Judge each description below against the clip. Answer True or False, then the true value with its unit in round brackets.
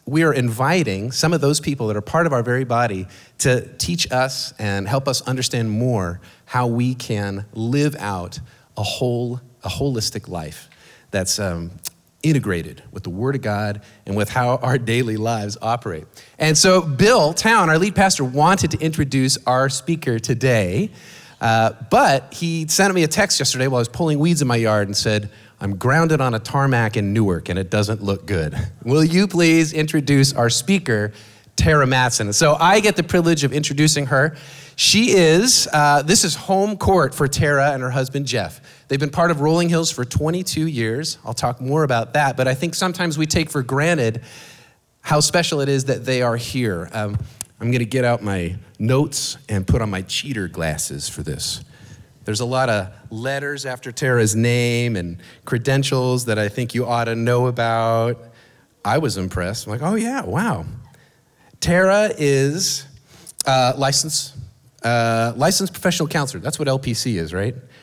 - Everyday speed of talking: True (180 wpm)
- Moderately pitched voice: False (130 Hz)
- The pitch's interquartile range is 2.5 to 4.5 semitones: False (5.1 semitones)